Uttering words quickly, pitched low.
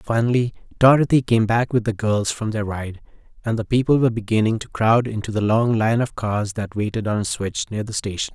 Yes: fast, 225 wpm; low, 110 Hz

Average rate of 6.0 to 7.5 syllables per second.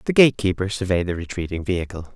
Yes: 7.0 syllables/s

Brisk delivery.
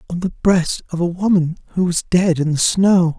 Yes: fast, 225 wpm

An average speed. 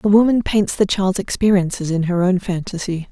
Yes: average, 195 wpm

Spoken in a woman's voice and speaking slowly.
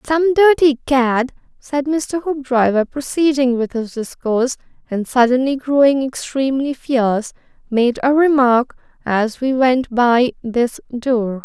Yes: female; slow, 125 wpm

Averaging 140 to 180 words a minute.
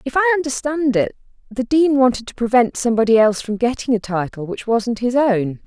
No: average, 200 wpm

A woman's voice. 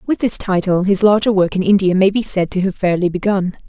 Yes: female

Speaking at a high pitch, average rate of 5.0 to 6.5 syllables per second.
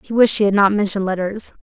No: high, 200 Hz; 6.9 syllables/s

